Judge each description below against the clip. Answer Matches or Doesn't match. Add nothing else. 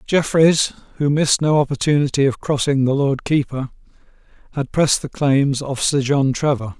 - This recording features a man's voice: Matches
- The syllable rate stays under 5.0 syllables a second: Doesn't match